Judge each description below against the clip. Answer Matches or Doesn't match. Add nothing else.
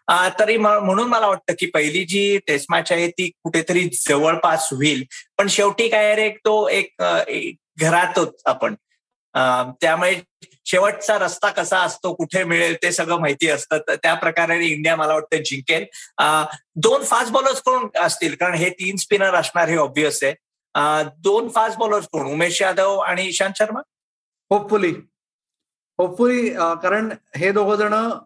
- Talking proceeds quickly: Matches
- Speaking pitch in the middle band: Matches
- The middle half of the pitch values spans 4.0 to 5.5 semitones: Matches